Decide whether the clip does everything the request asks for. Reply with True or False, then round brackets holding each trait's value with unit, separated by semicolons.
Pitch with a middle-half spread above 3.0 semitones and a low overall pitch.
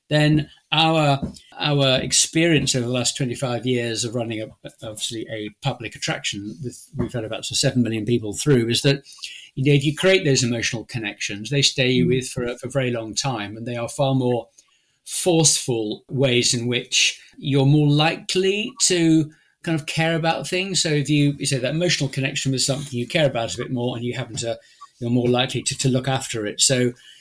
True (3.6 semitones; 130 Hz)